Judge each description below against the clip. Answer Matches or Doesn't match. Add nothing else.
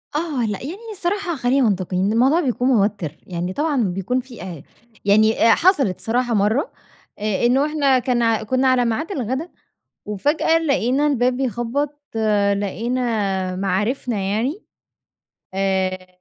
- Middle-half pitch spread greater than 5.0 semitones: Matches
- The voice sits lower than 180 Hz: Doesn't match